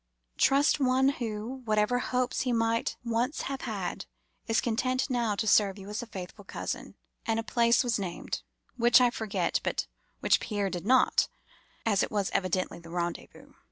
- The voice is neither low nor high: No, high, 225 Hz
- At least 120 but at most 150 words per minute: No, average, 170 wpm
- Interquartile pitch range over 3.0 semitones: Yes, average, 3.6 semitones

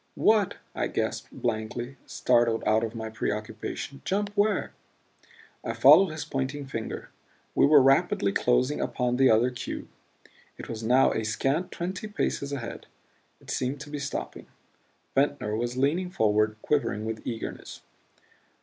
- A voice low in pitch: Yes, low, 130 Hz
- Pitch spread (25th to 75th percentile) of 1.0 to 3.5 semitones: No, average, 4.8 semitones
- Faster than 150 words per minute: No, average, 140 wpm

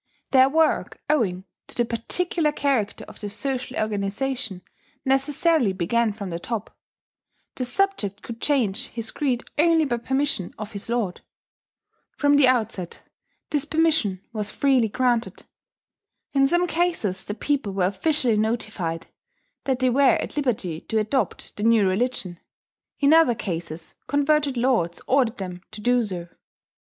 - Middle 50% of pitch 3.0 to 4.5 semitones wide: No, wide, 5.6 semitones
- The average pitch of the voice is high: Yes, high, 240 Hz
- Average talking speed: Yes, average, 145 wpm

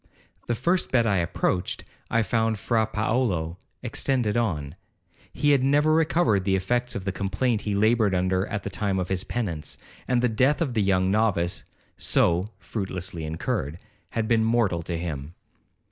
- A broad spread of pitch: No, average, 4.5 semitones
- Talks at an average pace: Yes, average, 165 wpm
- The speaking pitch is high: No, low, 105 Hz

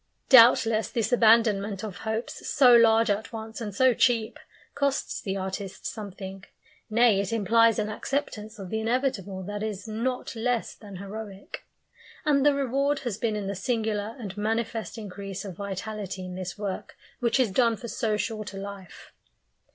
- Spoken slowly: No, average, 165 wpm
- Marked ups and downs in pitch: No, average, 2.7 semitones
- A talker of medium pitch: No, high, 220 Hz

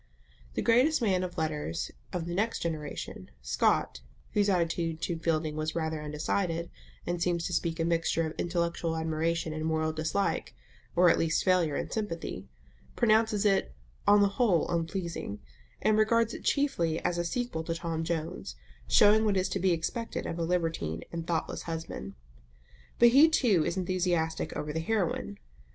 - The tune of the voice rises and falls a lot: No, average, 3.5 semitones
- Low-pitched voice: No, medium, 170 Hz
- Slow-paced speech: No, average, 165 wpm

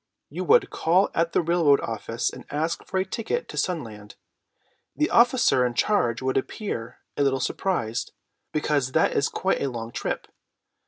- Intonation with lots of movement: Yes, wide, 7.8 semitones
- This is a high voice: No, medium, 145 Hz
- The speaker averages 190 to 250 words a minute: No, average, 165 wpm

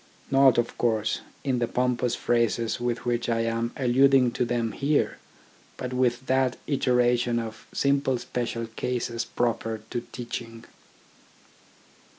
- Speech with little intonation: Yes, narrow, 1.5 semitones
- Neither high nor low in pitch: No, low, 120 Hz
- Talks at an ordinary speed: No, slow, 130 wpm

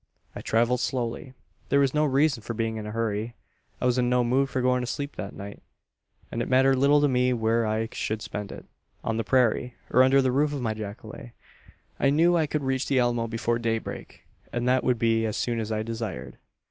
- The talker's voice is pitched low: Yes, low, 120 Hz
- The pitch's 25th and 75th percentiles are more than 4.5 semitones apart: No, average, 2.8 semitones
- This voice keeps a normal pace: No, fast, 225 wpm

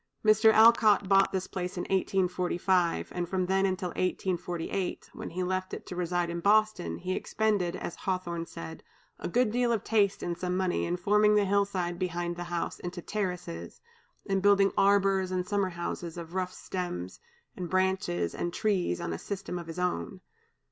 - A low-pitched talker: No, medium, 185 Hz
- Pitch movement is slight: Yes, narrow, 2.1 semitones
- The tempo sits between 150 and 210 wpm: Yes, average, 180 wpm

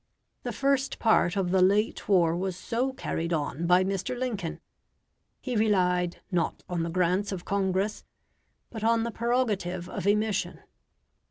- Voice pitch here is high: Yes, high, 195 Hz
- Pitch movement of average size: Yes, average, 3.8 semitones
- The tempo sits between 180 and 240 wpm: No, average, 150 wpm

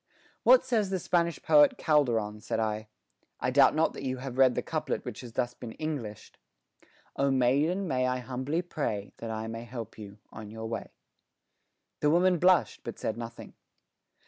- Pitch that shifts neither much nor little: No, wide, 6.3 semitones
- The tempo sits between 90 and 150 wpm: No, average, 175 wpm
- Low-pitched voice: Yes, low, 130 Hz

